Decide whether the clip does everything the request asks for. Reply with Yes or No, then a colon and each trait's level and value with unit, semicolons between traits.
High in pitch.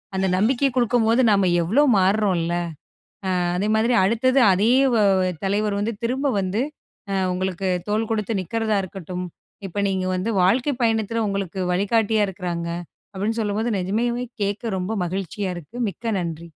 Yes: high, 205 Hz